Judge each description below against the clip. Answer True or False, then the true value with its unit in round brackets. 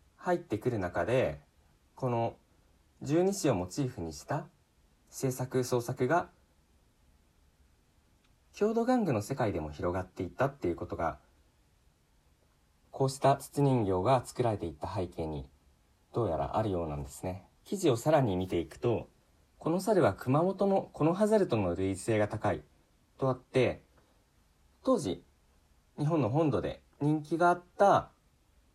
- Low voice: True (105 Hz)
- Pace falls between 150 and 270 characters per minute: True (265 characters per minute)